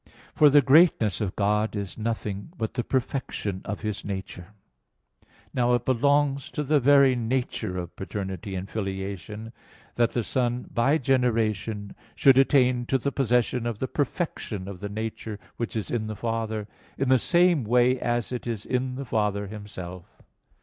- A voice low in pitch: Yes, low, 115 Hz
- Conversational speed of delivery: Yes, average, 165 wpm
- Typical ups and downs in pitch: Yes, average, 4.0 semitones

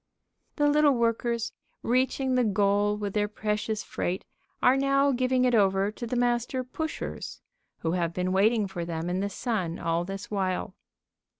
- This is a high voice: Yes, high, 215 Hz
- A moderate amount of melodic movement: Yes, average, 4.7 semitones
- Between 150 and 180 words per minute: Yes, average, 165 wpm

